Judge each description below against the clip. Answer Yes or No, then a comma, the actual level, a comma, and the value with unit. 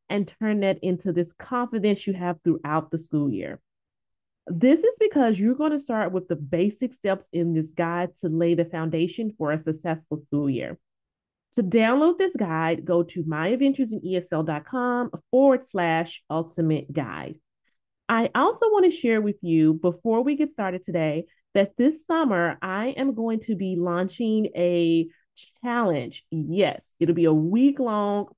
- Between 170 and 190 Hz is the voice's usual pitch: Yes, medium, 185 Hz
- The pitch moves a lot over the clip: Yes, wide, 6.2 semitones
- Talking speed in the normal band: Yes, average, 160 wpm